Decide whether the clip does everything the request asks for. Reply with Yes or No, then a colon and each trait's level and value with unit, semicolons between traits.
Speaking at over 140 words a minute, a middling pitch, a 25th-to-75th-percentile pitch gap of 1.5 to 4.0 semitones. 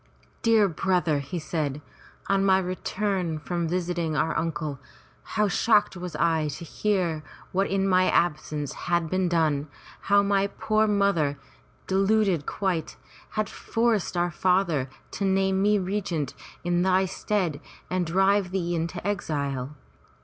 No: slow, 135 wpm; medium, 180 Hz; average, 3.4 semitones